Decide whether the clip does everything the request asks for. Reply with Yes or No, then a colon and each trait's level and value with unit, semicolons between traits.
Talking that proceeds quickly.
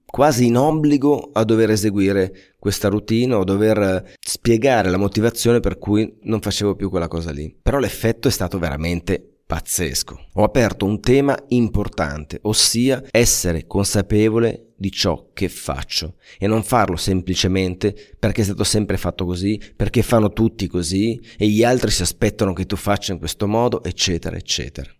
No: average, 160 wpm